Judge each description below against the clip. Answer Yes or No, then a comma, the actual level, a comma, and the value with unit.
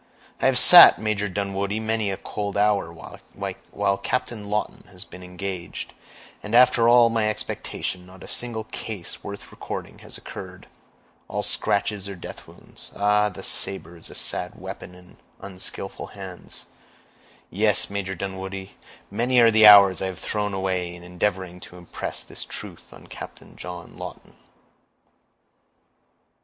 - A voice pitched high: No, low, 100 Hz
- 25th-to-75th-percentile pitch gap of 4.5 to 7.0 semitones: No, narrow, 2.4 semitones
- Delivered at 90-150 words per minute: Yes, average, 145 wpm